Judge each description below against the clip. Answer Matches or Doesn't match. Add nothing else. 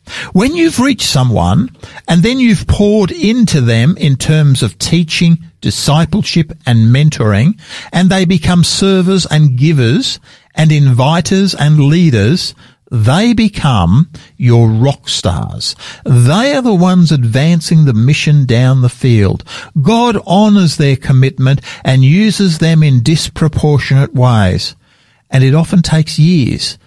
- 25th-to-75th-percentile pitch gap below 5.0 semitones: Doesn't match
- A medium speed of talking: Doesn't match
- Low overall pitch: Doesn't match